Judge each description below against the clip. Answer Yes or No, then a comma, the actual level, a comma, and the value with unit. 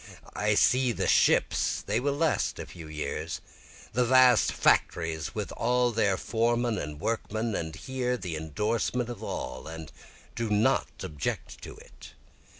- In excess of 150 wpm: No, average, 145 wpm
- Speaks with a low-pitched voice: Yes, low, 110 Hz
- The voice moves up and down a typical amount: No, wide, 7.2 semitones